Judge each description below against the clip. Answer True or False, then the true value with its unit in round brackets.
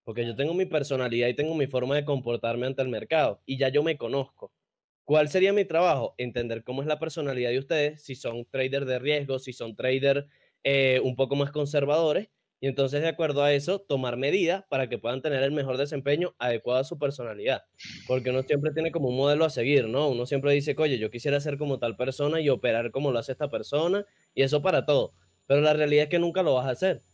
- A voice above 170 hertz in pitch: False (140 Hz)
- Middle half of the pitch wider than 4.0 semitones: False (2.8 semitones)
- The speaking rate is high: True (230 wpm)